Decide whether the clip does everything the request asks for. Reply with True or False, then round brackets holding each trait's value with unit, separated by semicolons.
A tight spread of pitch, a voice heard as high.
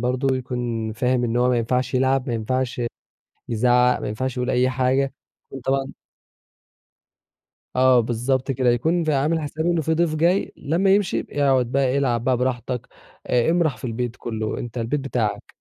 False (2.1 semitones; 130 Hz)